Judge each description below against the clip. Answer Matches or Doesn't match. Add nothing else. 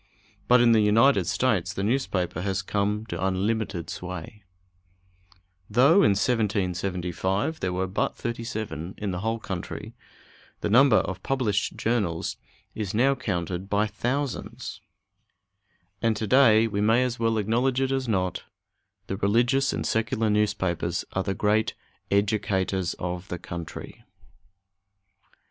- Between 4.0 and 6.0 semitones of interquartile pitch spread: Doesn't match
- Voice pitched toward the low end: Matches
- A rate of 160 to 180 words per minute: Doesn't match